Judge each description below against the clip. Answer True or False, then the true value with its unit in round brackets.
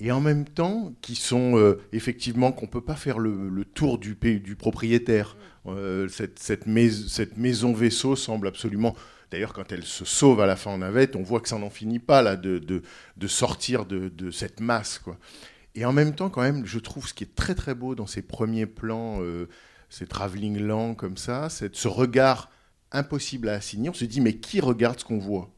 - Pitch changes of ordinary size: True (3.5 semitones)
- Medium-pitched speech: False (115 Hz)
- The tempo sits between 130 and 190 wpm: False (220 wpm)